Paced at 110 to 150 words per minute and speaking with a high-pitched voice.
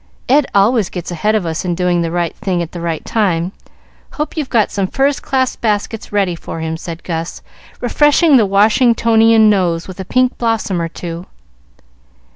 No: average, 180 wpm; high, 200 Hz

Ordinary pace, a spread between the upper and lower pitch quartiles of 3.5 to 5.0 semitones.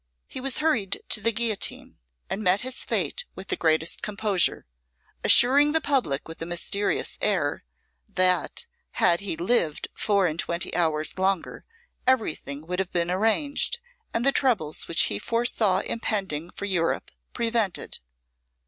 No: average, 145 wpm; wide, 5.5 semitones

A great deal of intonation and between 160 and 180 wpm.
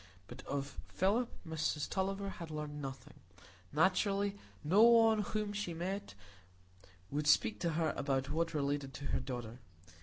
No: wide, 5.8 semitones; average, 145 wpm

